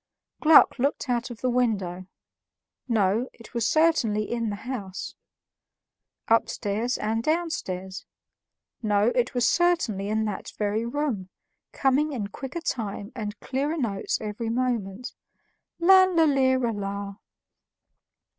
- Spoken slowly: Yes, slow, 115 wpm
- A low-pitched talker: No, high, 235 Hz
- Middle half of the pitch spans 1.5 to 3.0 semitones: No, average, 4.6 semitones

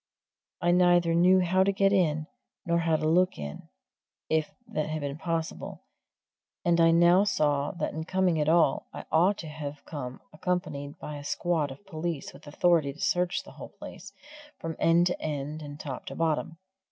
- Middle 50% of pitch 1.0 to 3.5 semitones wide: Yes, average, 2.8 semitones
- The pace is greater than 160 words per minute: Yes, average, 185 wpm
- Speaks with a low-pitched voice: No, medium, 165 Hz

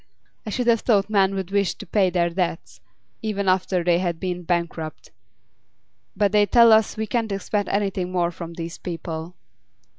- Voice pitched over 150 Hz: Yes, high, 190 Hz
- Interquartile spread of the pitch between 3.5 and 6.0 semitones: No, average, 3.1 semitones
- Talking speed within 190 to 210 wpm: No, average, 175 wpm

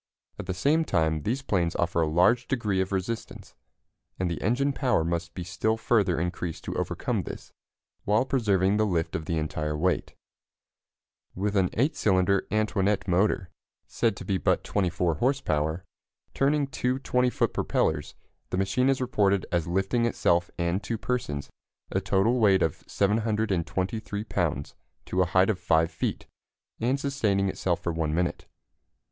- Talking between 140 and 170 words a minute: Yes, average, 160 wpm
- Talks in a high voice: No, very low, 95 Hz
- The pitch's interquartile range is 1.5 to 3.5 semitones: No, average, 4.7 semitones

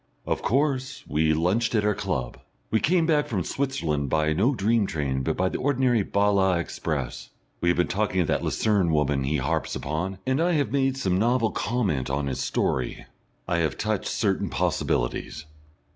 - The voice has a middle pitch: No, very low, 95 Hz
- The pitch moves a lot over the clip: Yes, wide, 7.5 semitones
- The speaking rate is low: No, average, 180 wpm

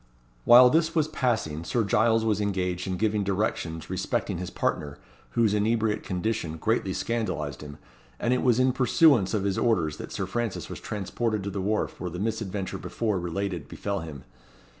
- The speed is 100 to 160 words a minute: No, average, 175 wpm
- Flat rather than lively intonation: No, average, 3.9 semitones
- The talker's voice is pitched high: No, low, 100 Hz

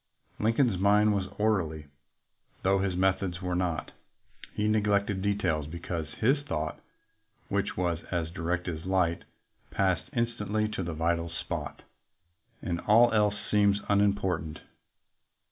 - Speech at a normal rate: No, slow, 125 wpm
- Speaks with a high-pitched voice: No, very low, 95 Hz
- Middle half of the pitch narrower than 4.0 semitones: Yes, average, 3.5 semitones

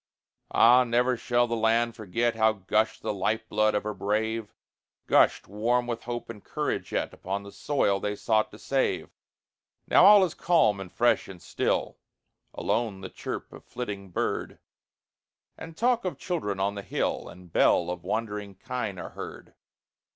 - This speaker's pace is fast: No, average, 165 wpm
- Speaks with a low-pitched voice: Yes, low, 110 Hz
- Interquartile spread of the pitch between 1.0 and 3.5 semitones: Yes, average, 3.2 semitones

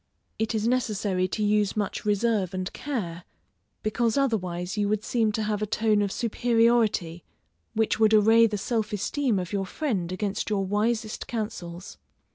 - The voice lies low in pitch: No, high, 210 Hz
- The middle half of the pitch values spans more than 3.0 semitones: No, average, 2.7 semitones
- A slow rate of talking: No, average, 160 wpm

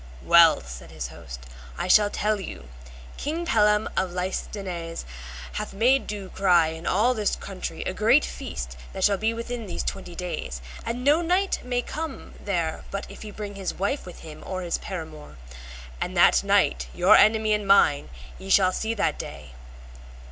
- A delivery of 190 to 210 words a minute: No, average, 175 wpm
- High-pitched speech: Yes, high, 195 Hz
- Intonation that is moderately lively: Yes, average, 4.1 semitones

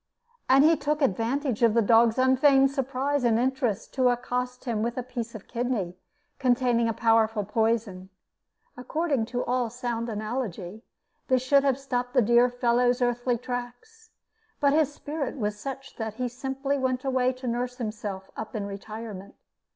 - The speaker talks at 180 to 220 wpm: No, average, 160 wpm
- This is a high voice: Yes, high, 245 Hz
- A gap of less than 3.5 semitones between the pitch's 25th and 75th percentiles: Yes, narrow, 2.6 semitones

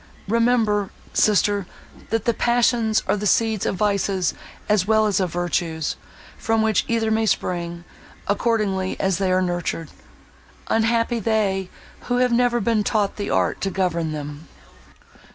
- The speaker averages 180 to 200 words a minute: No, average, 145 wpm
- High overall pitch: Yes, high, 205 Hz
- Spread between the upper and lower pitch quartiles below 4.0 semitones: Yes, average, 3.4 semitones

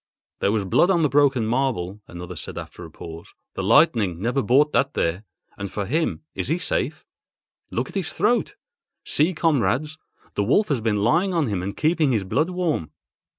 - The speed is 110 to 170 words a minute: No, average, 180 wpm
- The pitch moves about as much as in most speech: No, wide, 7.6 semitones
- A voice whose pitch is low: Yes, low, 130 Hz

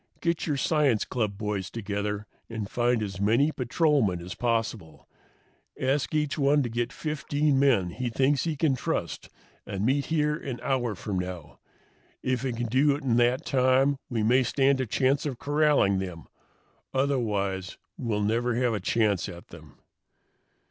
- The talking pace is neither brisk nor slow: Yes, average, 160 wpm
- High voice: No, low, 120 Hz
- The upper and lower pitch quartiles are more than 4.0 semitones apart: Yes, average, 5.0 semitones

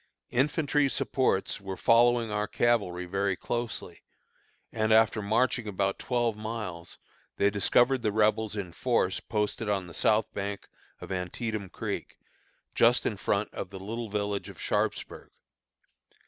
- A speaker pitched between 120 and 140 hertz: No, low, 105 Hz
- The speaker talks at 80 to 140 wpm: Yes, slow, 135 wpm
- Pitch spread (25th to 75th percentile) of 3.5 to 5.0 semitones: No, average, 3.0 semitones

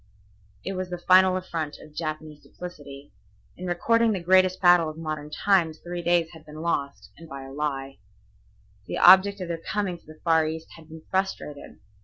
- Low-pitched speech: No, medium, 165 Hz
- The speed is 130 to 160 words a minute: No, average, 185 wpm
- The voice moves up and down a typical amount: Yes, average, 3.1 semitones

